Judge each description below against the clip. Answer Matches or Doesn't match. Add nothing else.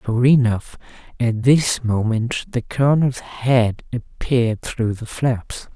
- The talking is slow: Matches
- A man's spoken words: Doesn't match